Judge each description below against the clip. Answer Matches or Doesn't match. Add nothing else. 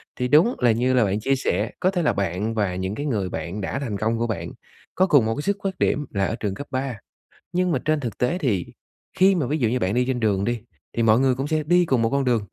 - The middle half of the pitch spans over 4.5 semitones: Matches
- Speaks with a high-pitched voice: Doesn't match